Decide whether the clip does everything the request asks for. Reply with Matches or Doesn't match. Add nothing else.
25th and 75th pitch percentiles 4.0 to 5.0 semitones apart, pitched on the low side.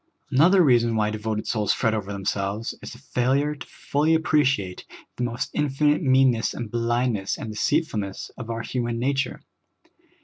Matches